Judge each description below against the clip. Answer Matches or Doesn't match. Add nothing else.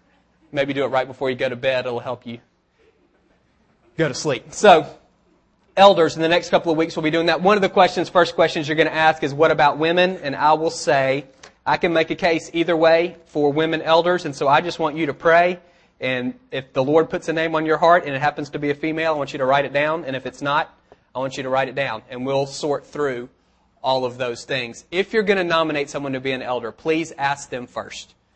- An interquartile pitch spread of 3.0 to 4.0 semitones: Matches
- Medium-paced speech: Doesn't match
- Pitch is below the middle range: Doesn't match